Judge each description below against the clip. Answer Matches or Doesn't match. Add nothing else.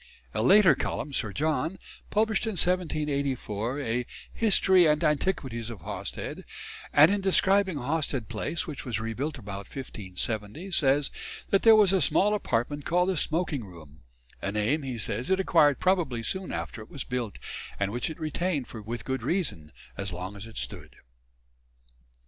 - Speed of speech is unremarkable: Matches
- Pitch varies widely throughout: Matches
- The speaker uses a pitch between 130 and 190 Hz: Matches